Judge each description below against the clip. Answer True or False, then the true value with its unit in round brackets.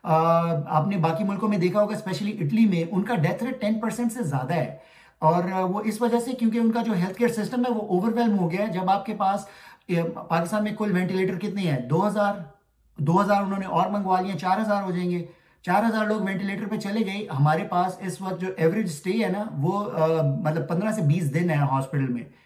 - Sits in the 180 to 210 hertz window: True (190 Hz)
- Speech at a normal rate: False (220 wpm)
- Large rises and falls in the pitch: False (4.2 semitones)